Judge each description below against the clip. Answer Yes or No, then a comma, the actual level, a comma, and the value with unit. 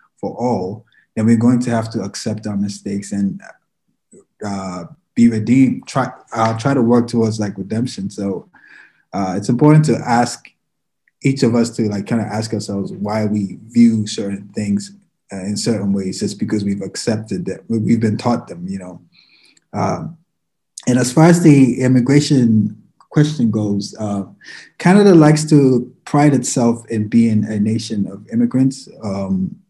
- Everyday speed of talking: Yes, average, 160 wpm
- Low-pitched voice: Yes, low, 115 Hz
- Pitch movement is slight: No, average, 3.8 semitones